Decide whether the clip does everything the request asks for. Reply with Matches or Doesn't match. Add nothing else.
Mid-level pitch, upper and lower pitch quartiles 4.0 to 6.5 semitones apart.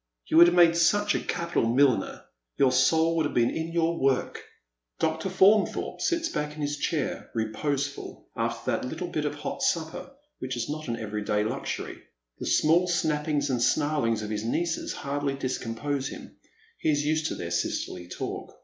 Matches